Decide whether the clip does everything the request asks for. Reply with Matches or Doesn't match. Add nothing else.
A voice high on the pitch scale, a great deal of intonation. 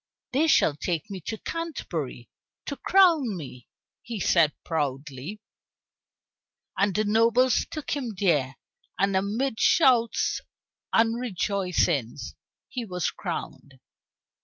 Matches